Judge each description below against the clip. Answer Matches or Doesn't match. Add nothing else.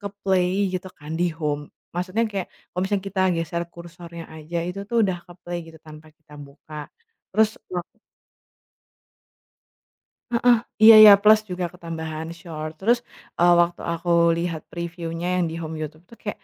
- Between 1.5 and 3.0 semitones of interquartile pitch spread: Matches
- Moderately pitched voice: Matches